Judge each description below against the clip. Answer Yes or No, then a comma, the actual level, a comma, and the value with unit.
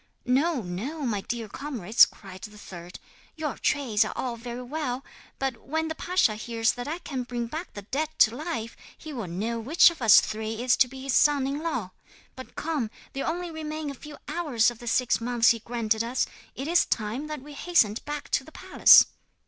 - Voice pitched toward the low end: No, very high, 250 Hz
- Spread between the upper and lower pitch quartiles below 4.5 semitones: No, average, 5.0 semitones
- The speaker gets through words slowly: No, fast, 205 wpm